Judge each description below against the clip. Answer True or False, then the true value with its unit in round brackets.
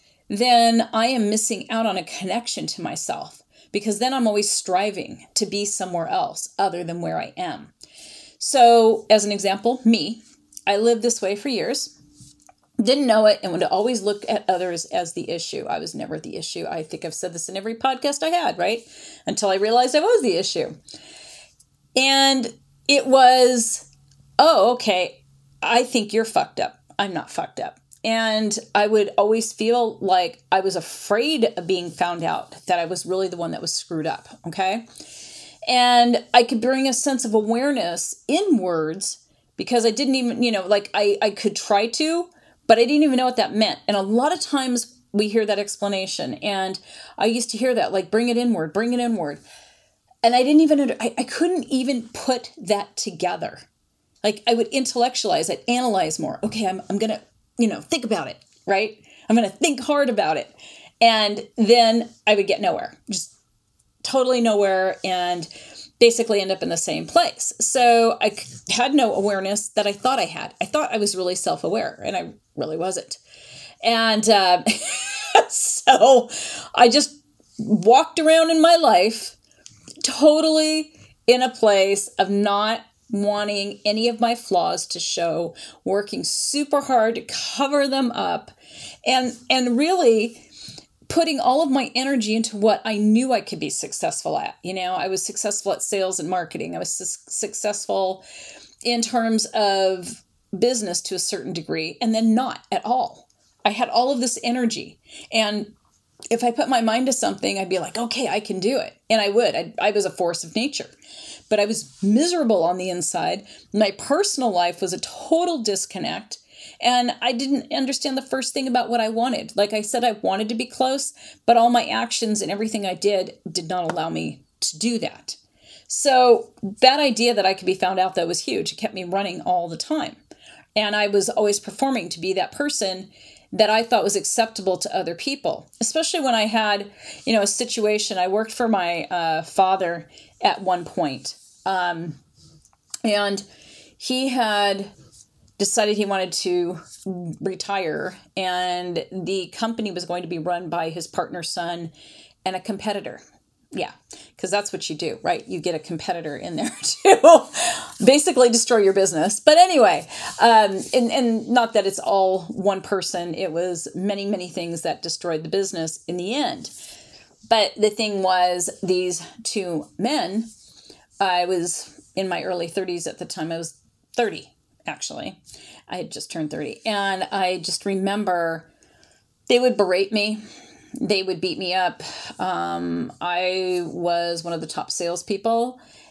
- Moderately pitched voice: False (215 Hz)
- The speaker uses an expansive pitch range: False (4.5 semitones)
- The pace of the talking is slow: False (175 wpm)